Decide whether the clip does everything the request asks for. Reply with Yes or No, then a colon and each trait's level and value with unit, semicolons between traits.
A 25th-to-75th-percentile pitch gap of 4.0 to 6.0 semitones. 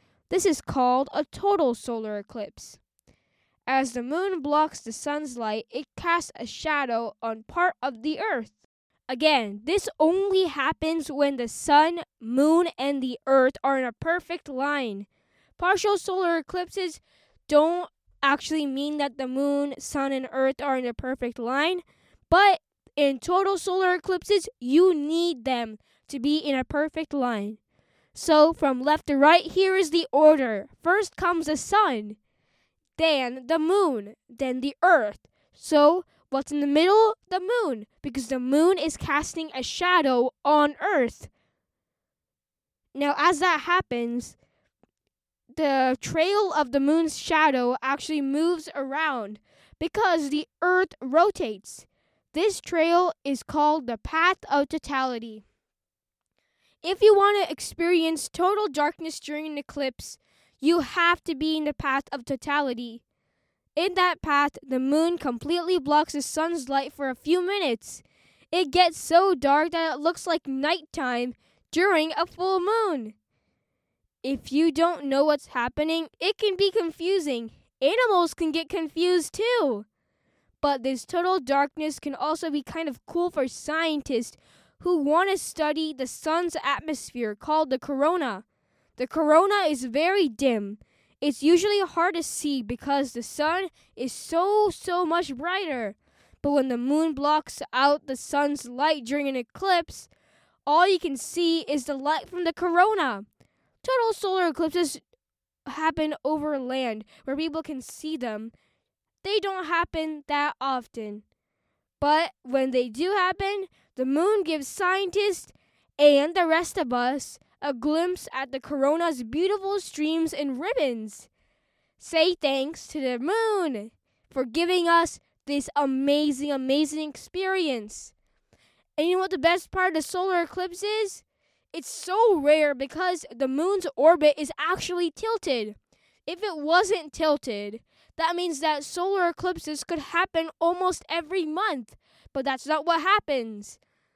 Yes: average, 4.5 semitones